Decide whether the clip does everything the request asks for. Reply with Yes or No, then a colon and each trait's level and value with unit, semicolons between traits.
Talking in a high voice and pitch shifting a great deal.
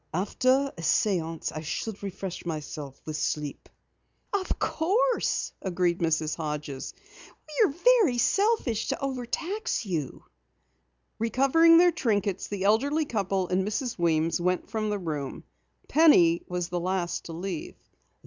Yes: high, 195 Hz; wide, 8.2 semitones